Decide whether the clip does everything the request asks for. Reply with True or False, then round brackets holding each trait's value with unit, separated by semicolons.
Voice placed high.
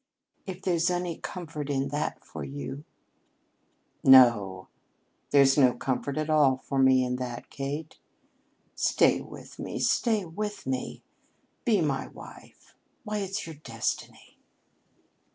False (145 Hz)